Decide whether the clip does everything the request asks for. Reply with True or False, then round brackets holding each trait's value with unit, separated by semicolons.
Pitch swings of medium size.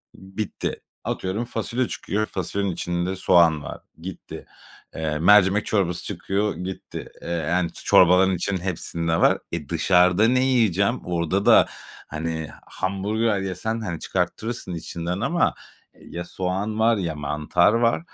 True (3.5 semitones)